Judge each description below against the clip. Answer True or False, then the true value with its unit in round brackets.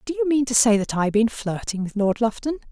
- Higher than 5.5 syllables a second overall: True (6.0 syllables/s)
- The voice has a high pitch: True (235 Hz)